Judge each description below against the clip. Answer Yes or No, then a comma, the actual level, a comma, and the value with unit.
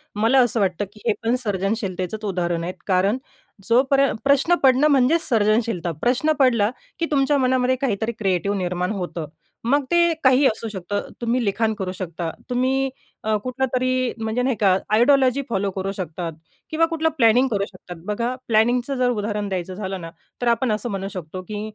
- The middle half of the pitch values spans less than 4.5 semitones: No, average, 4.9 semitones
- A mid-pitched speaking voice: No, high, 220 Hz